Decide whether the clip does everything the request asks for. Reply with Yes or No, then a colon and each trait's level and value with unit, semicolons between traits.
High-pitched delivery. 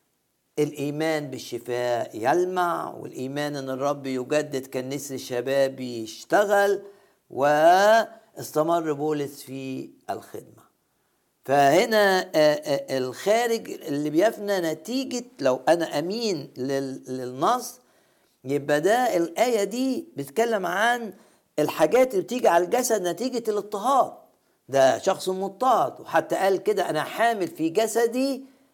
No: medium, 165 Hz